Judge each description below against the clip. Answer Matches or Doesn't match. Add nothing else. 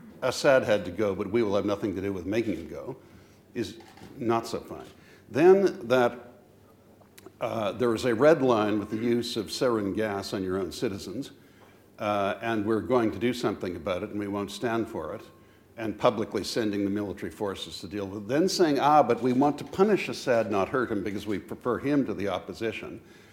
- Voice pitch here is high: Doesn't match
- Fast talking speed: Matches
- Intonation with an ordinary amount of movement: Matches